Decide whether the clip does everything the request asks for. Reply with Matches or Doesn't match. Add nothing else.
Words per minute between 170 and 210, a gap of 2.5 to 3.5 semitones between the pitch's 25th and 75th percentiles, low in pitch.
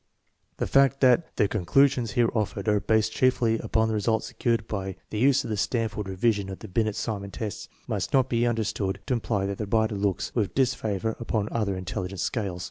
Matches